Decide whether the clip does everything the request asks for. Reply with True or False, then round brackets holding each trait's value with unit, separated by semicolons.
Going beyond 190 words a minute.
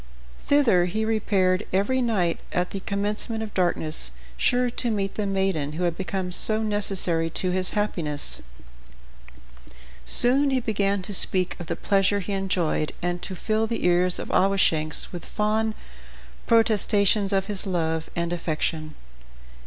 False (145 wpm)